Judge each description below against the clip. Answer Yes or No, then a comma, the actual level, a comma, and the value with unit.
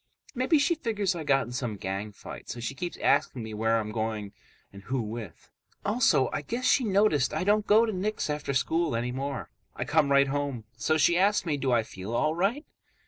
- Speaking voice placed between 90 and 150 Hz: Yes, medium, 140 Hz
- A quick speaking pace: Yes, fast, 210 wpm